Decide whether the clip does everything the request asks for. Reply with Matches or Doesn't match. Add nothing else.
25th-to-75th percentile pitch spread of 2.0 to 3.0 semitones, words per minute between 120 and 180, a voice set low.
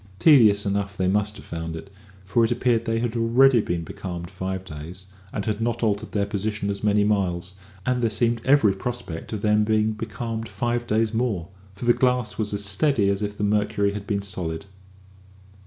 Doesn't match